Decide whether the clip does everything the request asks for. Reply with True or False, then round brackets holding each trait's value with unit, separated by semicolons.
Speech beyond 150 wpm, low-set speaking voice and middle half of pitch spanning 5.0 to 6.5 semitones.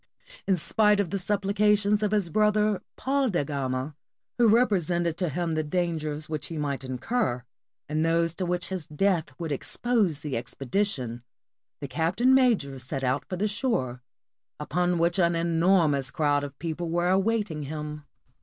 False (160 wpm; 170 Hz; 5.4 semitones)